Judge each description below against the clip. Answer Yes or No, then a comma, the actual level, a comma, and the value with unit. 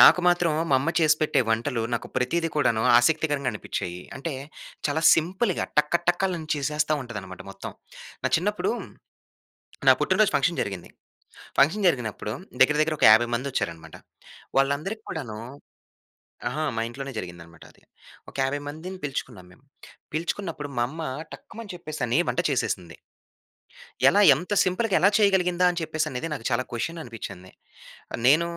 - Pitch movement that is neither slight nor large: No, wide, 6.2 semitones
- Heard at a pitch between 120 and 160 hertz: Yes, medium, 150 Hz